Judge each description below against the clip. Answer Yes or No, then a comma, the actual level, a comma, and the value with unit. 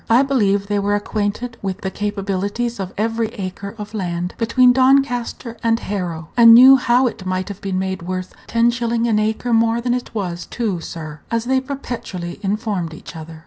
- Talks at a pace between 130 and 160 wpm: No, average, 185 wpm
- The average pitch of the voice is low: No, high, 210 Hz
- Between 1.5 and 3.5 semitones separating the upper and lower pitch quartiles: No, average, 4.0 semitones